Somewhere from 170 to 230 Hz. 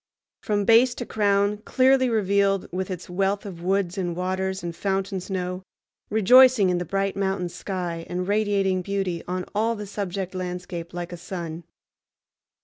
Yes: high, 190 Hz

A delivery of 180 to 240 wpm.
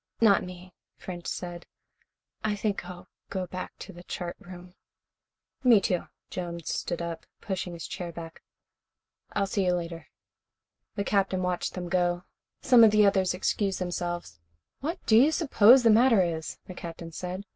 No: average, 160 wpm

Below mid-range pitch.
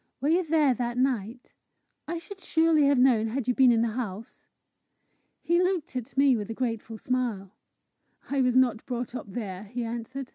No: very high, 250 Hz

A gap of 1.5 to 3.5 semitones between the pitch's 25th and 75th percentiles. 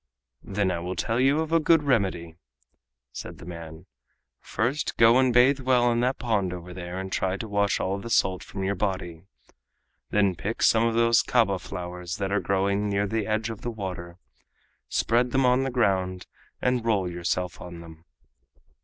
No: average, 4.6 semitones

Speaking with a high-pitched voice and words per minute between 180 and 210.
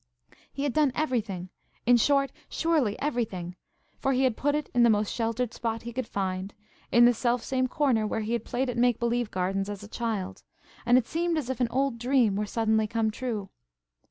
Yes: high, 235 Hz; average, 200 wpm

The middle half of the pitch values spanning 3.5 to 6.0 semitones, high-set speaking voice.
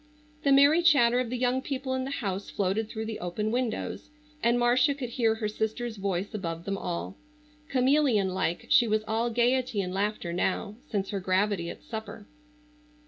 Yes: average, 4.2 semitones; high, 220 Hz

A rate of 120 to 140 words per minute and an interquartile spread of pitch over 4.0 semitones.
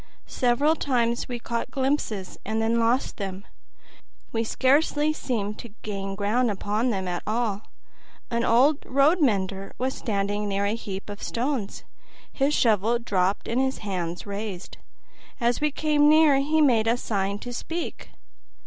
No: average, 150 wpm; average, 4.7 semitones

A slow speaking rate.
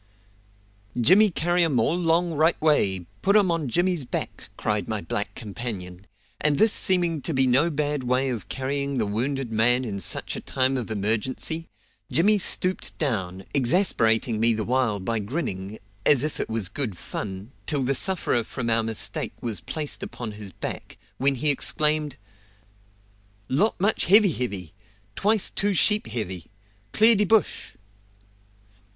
No: average, 155 wpm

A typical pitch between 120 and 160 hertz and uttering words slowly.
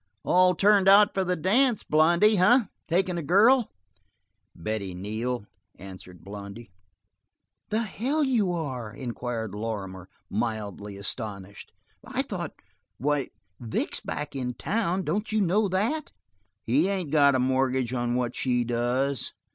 Yes: low, 135 Hz; slow, 130 wpm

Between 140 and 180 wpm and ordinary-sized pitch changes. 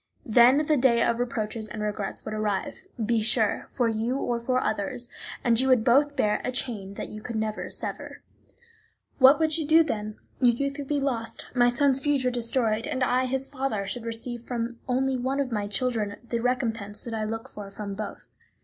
No: average, 200 wpm; average, 3.3 semitones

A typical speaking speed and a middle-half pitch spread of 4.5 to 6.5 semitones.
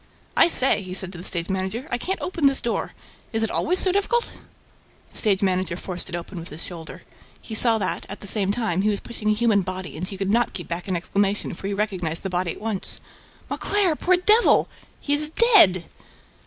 No: fast, 220 wpm; average, 4.9 semitones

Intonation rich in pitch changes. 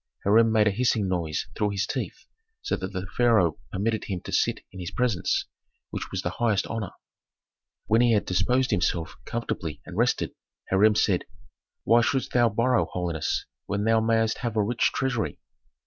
No: average, 3.7 semitones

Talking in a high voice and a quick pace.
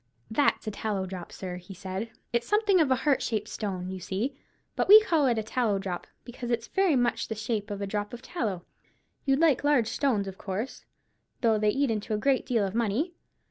Yes: high, 225 Hz; fast, 220 wpm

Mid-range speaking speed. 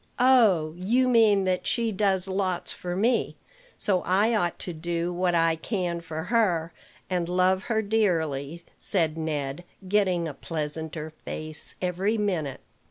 Yes: average, 145 wpm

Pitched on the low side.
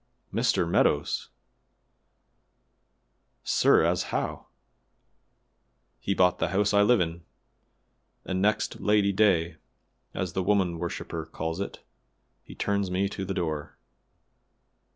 Yes: very low, 95 Hz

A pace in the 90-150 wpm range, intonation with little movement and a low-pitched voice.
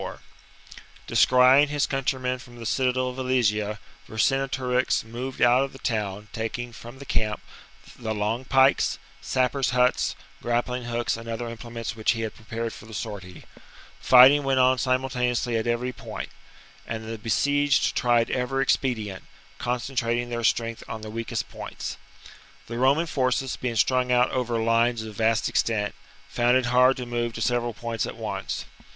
No: average, 170 wpm; narrow, 2.1 semitones; low, 120 Hz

